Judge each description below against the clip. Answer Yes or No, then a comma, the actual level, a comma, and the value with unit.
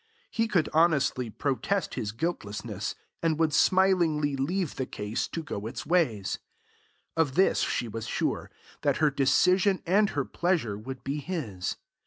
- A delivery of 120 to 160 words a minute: Yes, average, 150 wpm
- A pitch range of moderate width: No, wide, 7.0 semitones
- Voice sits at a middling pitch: Yes, medium, 150 Hz